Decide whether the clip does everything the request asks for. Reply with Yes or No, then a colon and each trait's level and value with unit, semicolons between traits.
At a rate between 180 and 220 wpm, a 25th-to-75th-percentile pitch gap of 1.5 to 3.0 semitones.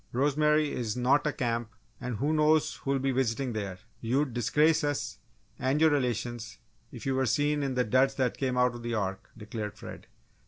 No: average, 190 wpm; average, 3.6 semitones